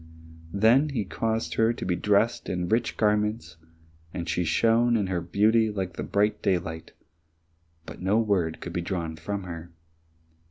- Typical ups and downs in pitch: Yes, average, 4.3 semitones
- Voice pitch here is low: Yes, low, 100 Hz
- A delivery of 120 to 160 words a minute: Yes, average, 155 wpm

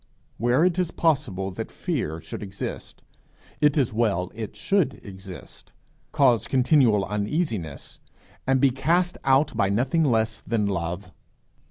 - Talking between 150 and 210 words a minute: No, slow, 135 wpm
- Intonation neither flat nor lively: No, wide, 6.1 semitones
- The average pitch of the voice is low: Yes, low, 115 Hz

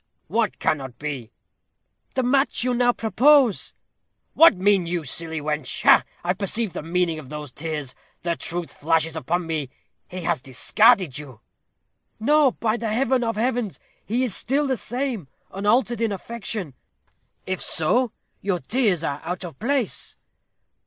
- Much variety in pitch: Yes, wide, 6.8 semitones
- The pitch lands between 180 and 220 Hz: Yes, high, 190 Hz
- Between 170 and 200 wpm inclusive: No, average, 150 wpm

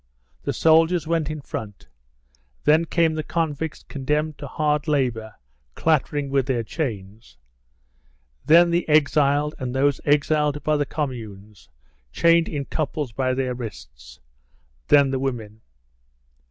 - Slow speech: Yes, slow, 125 wpm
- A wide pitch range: No, average, 3.6 semitones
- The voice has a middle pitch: Yes, medium, 145 Hz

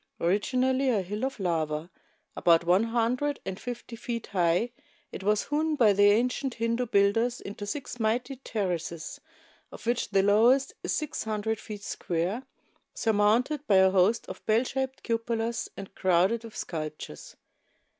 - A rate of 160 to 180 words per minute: No, average, 150 wpm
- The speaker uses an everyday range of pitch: Yes, average, 4.2 semitones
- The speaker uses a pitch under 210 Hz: No, high, 220 Hz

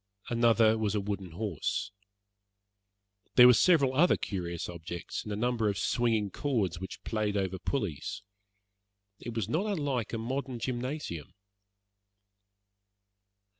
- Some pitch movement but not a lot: Yes, average, 4.4 semitones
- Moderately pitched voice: No, low, 110 Hz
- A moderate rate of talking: No, slow, 125 wpm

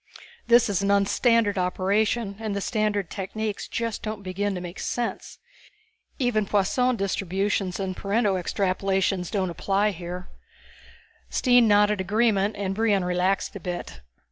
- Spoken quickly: No, average, 140 wpm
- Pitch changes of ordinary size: No, narrow, 2.3 semitones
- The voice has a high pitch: Yes, high, 200 Hz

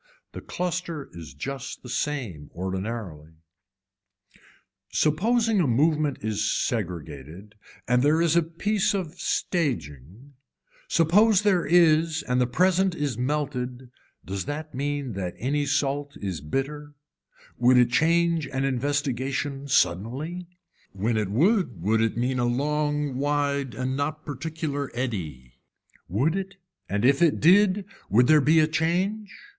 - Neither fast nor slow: No, slow, 130 wpm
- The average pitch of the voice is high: No, medium, 140 Hz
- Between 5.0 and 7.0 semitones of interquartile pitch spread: Yes, average, 5.3 semitones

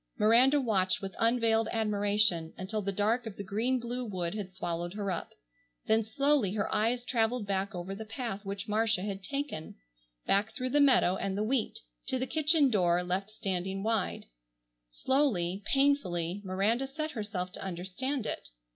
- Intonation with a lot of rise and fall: No, average, 4.3 semitones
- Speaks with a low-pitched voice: No, high, 210 Hz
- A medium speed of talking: Yes, average, 165 wpm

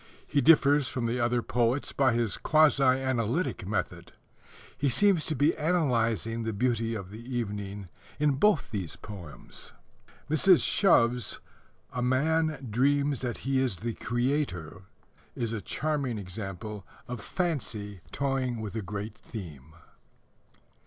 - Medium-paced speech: No, slow, 130 wpm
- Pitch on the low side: Yes, low, 120 Hz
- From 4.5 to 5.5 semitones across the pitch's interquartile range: Yes, average, 4.9 semitones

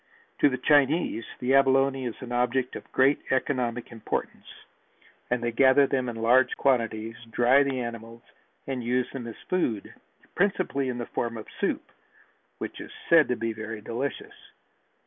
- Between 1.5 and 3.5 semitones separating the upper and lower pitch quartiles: Yes, narrow, 2.6 semitones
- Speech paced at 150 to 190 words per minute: Yes, average, 160 wpm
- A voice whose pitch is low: Yes, low, 125 Hz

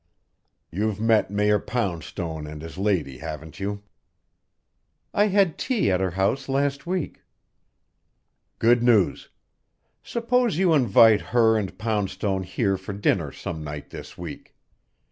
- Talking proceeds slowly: Yes, slow, 125 wpm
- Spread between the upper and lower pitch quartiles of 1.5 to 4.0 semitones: No, average, 5.3 semitones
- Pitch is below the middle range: Yes, low, 105 Hz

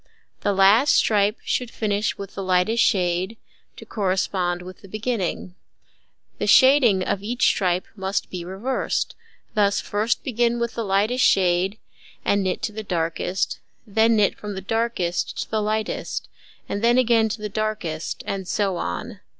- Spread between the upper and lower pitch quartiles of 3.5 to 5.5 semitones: No, average, 3.1 semitones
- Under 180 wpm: Yes, average, 160 wpm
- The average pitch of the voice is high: Yes, high, 205 Hz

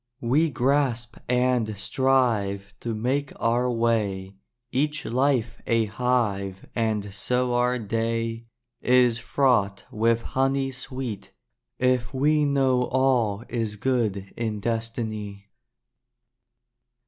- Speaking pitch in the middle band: No, low, 120 Hz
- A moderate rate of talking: No, slow, 100 wpm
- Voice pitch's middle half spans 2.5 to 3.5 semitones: Yes, average, 2.9 semitones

